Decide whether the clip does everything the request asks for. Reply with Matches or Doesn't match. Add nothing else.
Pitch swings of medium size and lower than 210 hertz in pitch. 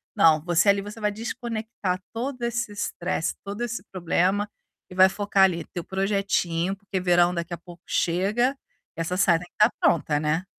Matches